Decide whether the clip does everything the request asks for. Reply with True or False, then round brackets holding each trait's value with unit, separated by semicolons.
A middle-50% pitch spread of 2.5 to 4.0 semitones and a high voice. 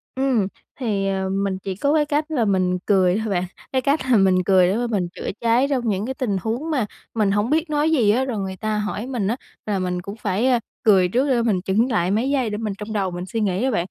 False (4.8 semitones; 215 Hz)